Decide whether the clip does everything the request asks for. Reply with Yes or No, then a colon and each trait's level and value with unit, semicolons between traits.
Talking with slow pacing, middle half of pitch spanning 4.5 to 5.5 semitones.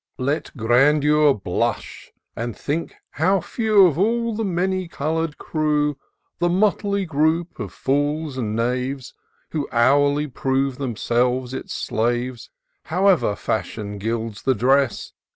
Yes: slow, 120 wpm; average, 5.2 semitones